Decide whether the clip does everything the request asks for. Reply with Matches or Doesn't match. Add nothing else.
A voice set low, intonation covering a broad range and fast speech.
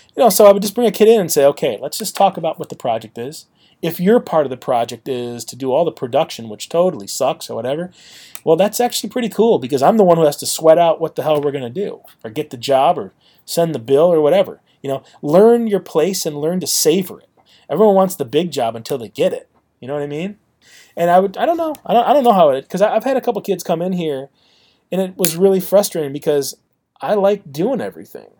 Doesn't match